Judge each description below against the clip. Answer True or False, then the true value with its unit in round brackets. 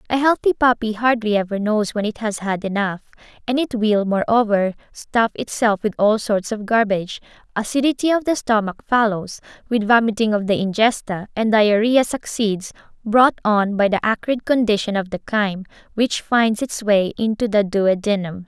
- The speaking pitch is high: True (215 Hz)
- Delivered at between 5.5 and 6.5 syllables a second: False (4.9 syllables/s)